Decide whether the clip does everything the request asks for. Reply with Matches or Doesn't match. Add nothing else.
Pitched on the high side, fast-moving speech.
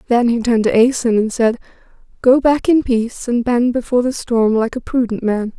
Matches